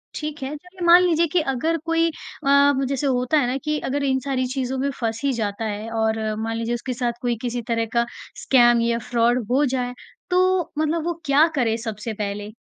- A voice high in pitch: Yes, very high, 255 Hz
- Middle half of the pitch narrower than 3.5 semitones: No, average, 4.5 semitones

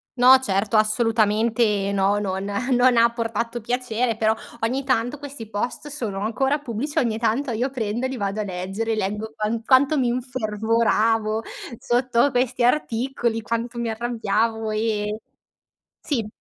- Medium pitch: No, high, 230 Hz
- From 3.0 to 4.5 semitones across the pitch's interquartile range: No, narrow, 2.6 semitones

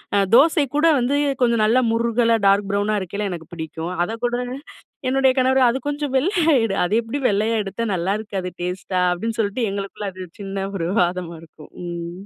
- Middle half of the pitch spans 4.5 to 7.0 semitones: Yes, average, 4.8 semitones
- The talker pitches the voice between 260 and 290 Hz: No, high, 210 Hz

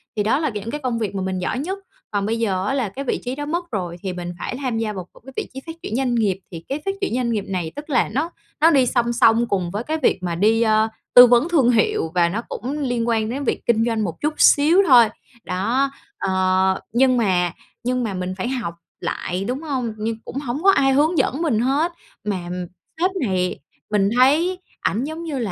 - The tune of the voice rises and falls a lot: Yes, wide, 5.8 semitones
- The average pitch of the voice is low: No, high, 235 Hz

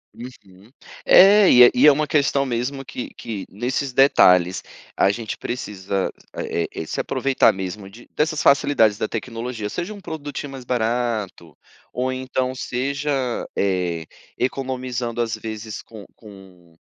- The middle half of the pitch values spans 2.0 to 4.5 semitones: No, average, 4.9 semitones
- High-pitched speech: No, low, 120 Hz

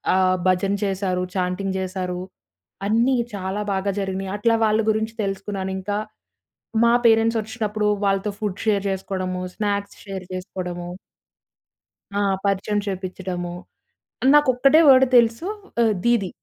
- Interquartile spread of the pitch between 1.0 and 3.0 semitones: Yes, average, 2.7 semitones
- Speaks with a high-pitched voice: Yes, high, 195 Hz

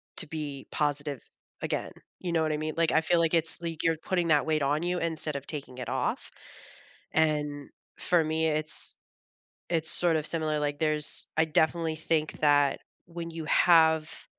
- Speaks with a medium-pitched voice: Yes, medium, 155 Hz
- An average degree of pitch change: No, narrow, 1.7 semitones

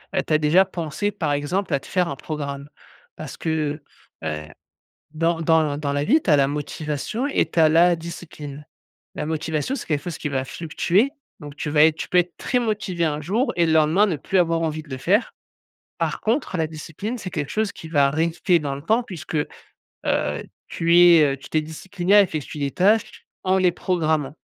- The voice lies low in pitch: No, medium, 160 Hz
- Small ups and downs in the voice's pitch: No, average, 3.5 semitones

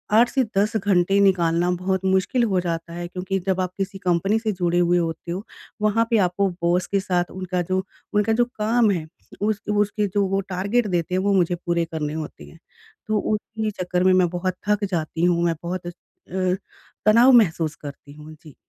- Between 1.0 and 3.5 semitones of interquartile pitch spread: Yes, average, 3.0 semitones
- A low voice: No, medium, 185 Hz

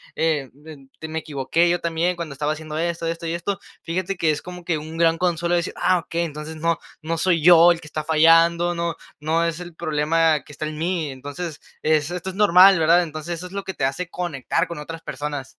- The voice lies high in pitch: No, medium, 165 Hz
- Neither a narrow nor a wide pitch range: No, narrow, 2.0 semitones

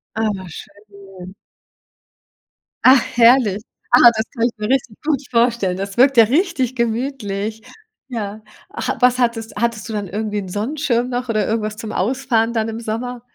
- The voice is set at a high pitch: Yes, high, 230 Hz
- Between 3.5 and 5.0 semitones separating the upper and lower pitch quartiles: No, average, 2.9 semitones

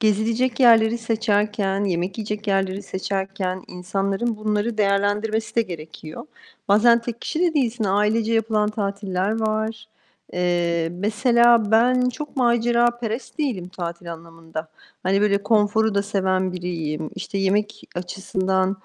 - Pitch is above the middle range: Yes, high, 205 Hz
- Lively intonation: No, average, 3.1 semitones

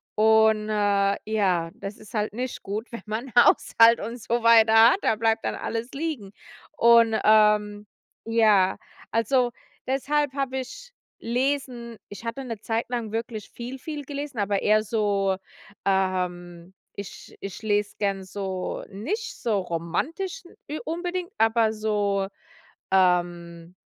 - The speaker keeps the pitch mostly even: No, average, 3.6 semitones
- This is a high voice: Yes, high, 220 Hz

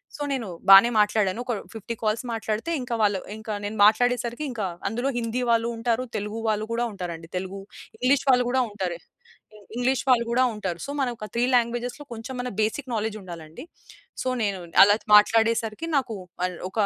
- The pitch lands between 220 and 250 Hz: Yes, high, 225 Hz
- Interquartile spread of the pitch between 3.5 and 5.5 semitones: No, average, 2.9 semitones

